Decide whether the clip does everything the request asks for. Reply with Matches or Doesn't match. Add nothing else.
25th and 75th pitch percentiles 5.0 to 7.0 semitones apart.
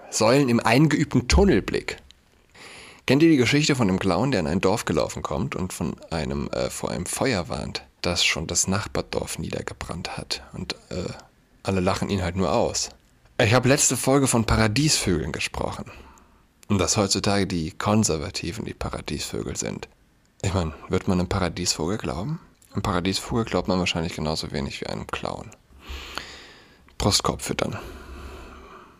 Matches